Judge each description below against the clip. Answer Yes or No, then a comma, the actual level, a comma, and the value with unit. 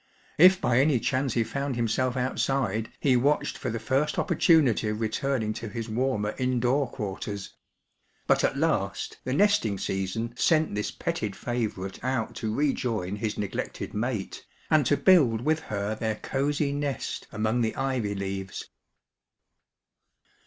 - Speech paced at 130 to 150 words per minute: Yes, average, 145 wpm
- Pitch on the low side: Yes, low, 120 Hz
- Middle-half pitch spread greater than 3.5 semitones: Yes, average, 4.3 semitones